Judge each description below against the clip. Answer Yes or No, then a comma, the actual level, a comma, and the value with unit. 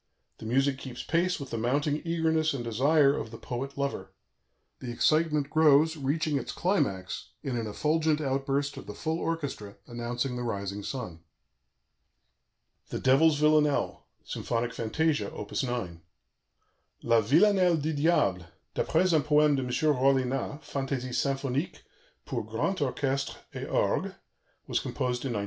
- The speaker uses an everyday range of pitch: Yes, average, 4.1 semitones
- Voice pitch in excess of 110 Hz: Yes, medium, 140 Hz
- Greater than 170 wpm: No, average, 140 wpm